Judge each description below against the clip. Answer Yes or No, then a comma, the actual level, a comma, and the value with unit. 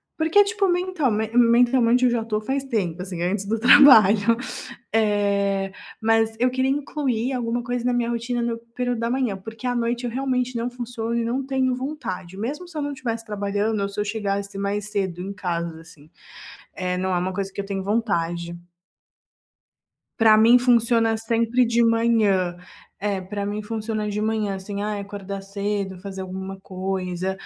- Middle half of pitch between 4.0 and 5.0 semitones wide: No, average, 3.6 semitones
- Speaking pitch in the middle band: No, high, 220 Hz